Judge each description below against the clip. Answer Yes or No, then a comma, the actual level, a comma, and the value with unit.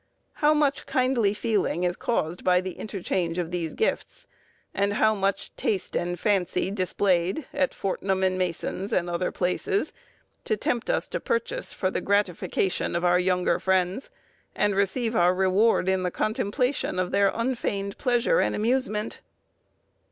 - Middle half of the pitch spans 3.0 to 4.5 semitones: Yes, average, 4.2 semitones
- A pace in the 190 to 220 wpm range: No, average, 150 wpm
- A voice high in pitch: Yes, high, 195 Hz